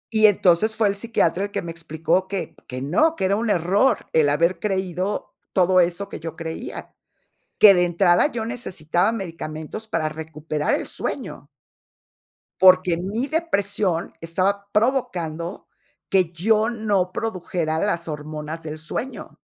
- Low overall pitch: No, medium, 180 Hz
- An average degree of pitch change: Yes, average, 3.9 semitones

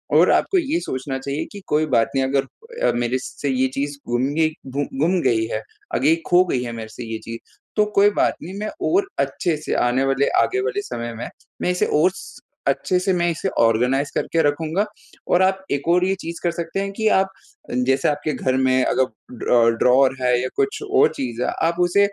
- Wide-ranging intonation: Yes, wide, 6.2 semitones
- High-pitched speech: No, medium, 145 Hz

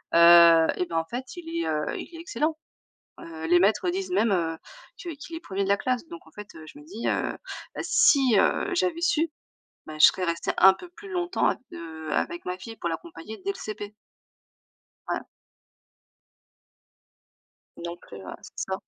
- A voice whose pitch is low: No, high, 205 Hz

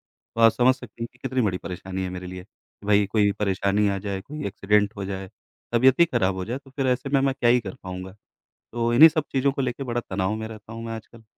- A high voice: No, low, 110 Hz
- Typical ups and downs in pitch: Yes, average, 4.3 semitones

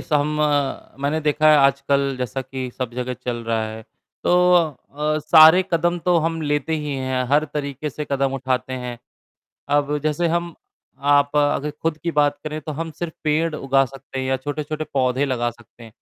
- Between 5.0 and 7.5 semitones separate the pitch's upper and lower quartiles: No, average, 2.8 semitones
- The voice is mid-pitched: Yes, medium, 145 Hz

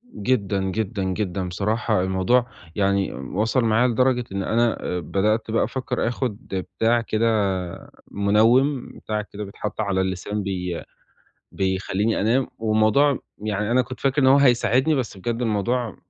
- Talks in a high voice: No, low, 110 Hz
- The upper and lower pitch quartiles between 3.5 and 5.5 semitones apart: Yes, average, 3.8 semitones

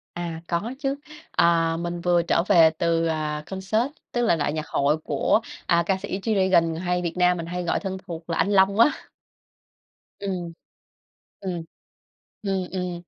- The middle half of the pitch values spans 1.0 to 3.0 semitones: Yes, narrow, 2.4 semitones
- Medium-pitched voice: Yes, medium, 175 Hz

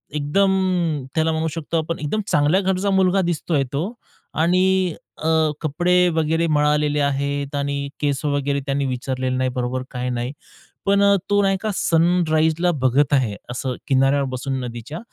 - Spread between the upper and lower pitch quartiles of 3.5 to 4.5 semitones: Yes, average, 4.0 semitones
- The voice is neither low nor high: Yes, medium, 150 Hz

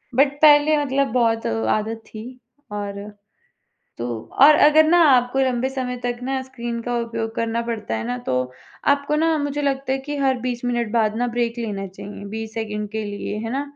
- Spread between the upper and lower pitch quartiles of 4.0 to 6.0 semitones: No, average, 3.6 semitones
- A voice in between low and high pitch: No, high, 240 Hz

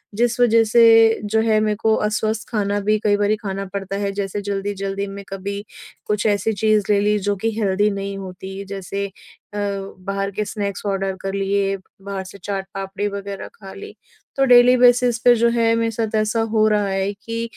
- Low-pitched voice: No, high, 205 Hz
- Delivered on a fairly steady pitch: Yes, narrow, 2.0 semitones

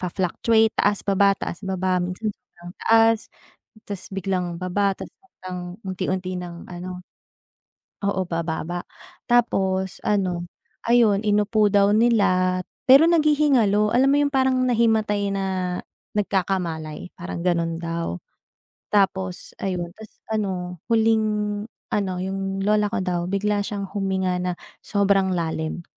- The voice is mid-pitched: No, high, 195 Hz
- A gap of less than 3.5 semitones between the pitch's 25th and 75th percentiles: Yes, average, 2.7 semitones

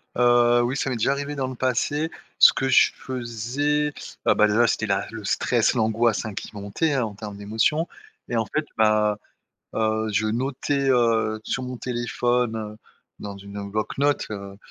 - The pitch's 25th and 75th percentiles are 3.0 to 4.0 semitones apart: Yes, average, 3.4 semitones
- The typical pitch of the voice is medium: No, low, 115 Hz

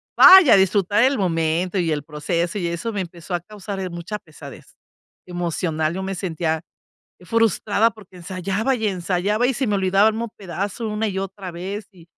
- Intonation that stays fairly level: No, average, 3.5 semitones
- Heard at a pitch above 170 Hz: Yes, high, 190 Hz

